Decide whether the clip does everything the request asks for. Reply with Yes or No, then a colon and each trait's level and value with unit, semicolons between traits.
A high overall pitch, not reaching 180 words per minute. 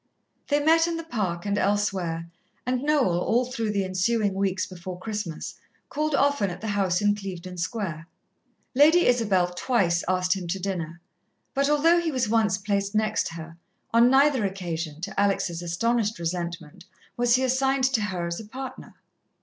Yes: high, 205 Hz; average, 165 wpm